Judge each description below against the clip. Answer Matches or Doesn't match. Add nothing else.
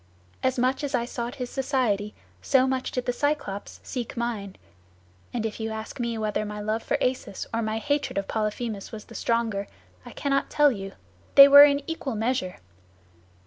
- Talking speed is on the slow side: Doesn't match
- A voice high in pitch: Matches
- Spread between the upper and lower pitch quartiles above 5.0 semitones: Doesn't match